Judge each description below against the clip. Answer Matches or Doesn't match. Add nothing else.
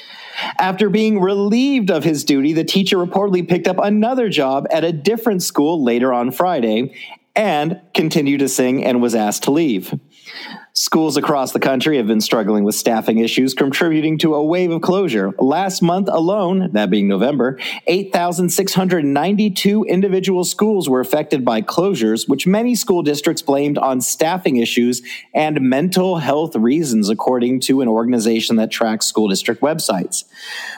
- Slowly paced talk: Doesn't match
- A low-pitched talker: Doesn't match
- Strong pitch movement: Matches